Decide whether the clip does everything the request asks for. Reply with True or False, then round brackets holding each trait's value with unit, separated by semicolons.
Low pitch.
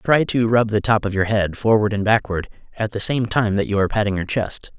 True (105 Hz)